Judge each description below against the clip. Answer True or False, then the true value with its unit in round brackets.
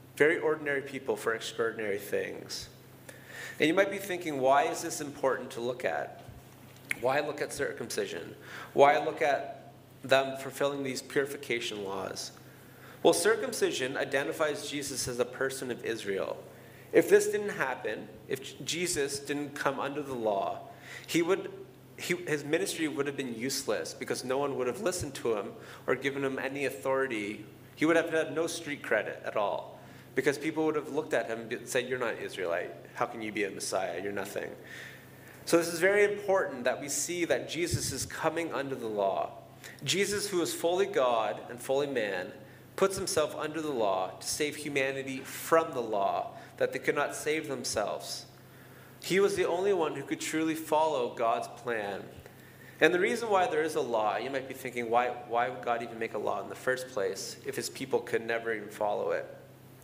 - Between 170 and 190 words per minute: True (185 wpm)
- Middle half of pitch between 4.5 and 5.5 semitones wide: True (4.8 semitones)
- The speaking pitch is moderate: True (145 Hz)